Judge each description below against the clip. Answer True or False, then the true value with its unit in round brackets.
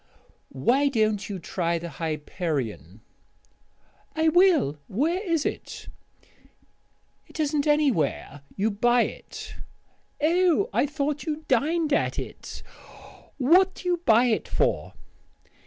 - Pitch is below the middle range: False (275 Hz)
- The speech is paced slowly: True (115 wpm)